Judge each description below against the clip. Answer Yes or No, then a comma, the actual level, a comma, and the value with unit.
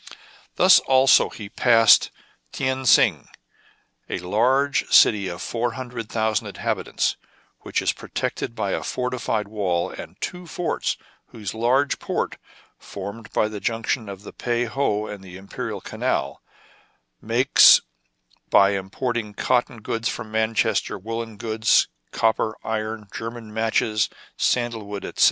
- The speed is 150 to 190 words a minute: No, slow, 135 wpm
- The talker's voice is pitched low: Yes, low, 110 Hz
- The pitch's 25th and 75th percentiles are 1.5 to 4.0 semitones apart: Yes, narrow, 2.4 semitones